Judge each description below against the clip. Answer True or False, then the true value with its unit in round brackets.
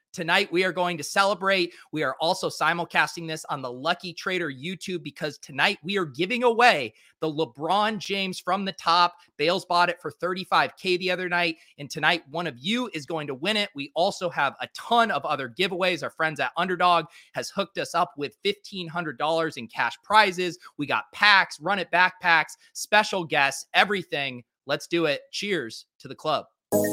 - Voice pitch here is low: False (175 Hz)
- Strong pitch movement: False (3.3 semitones)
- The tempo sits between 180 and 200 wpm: True (185 wpm)